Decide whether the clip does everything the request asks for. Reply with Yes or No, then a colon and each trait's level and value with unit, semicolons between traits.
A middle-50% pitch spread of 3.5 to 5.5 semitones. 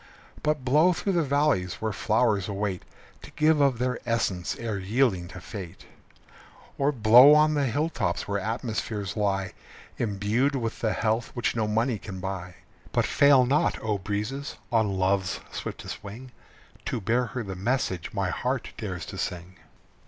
Yes: average, 5.1 semitones